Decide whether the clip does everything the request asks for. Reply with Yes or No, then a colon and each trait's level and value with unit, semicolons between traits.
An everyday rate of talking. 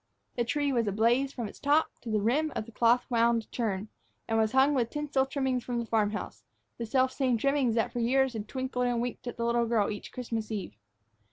No: fast, 225 wpm